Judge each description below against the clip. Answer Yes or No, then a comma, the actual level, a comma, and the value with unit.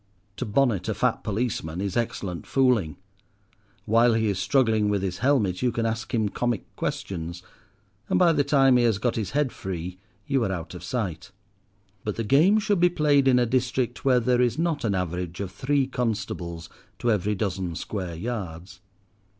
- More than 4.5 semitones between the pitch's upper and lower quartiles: Yes, wide, 5.5 semitones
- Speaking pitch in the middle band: No, low, 110 Hz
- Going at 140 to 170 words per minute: No, average, 180 wpm